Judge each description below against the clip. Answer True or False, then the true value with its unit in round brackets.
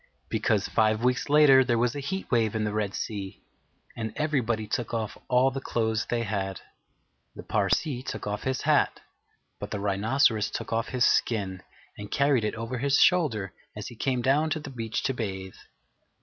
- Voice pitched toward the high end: False (115 Hz)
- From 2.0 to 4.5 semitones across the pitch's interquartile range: True (3.9 semitones)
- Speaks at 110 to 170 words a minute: False (185 wpm)